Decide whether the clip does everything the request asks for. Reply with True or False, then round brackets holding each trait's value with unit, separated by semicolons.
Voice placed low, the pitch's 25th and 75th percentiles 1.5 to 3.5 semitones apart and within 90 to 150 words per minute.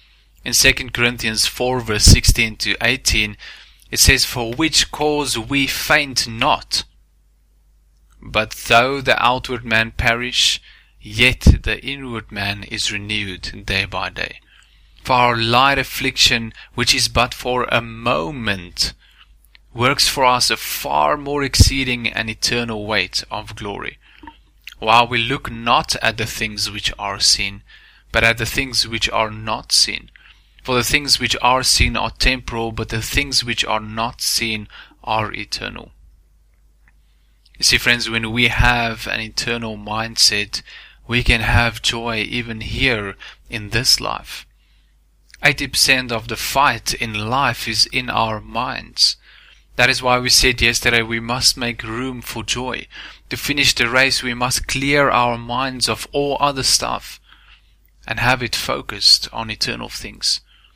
True (115 Hz; 2.6 semitones; 145 wpm)